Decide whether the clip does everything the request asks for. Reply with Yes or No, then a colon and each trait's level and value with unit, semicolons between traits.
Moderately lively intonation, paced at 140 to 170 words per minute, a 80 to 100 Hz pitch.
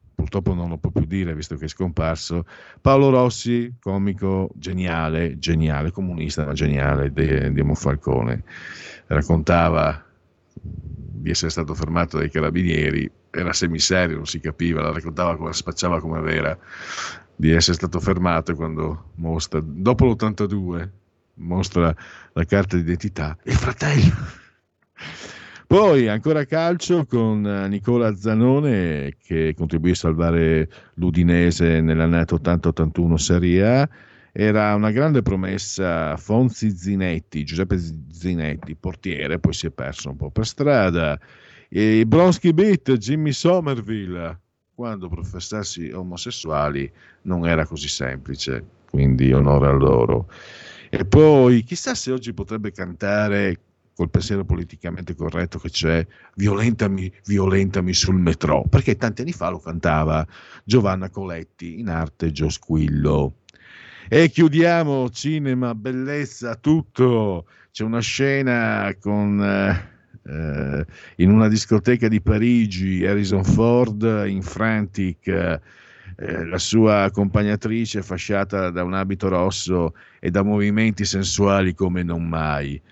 No: average, 4.8 semitones; average, 120 wpm; very low, 90 Hz